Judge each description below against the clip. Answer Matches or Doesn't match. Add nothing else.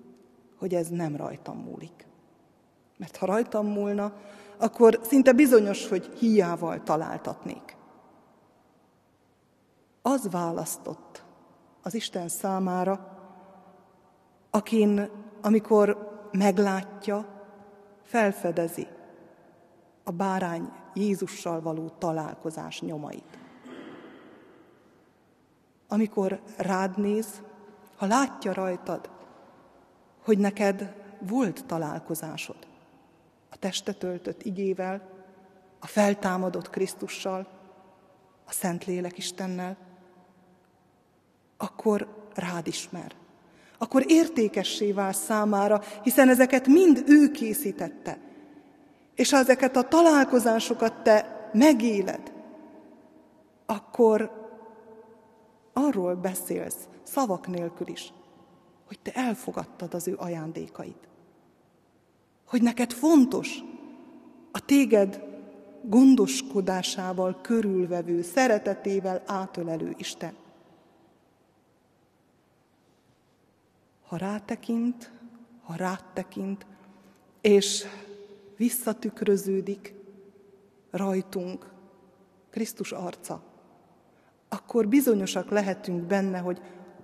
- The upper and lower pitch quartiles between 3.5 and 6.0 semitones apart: Doesn't match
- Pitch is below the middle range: Doesn't match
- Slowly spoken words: Matches